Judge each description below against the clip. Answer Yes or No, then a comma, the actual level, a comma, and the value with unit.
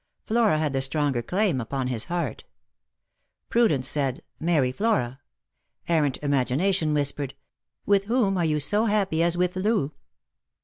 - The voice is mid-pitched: Yes, medium, 155 Hz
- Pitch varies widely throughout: Yes, wide, 6.3 semitones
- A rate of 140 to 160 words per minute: Yes, average, 150 wpm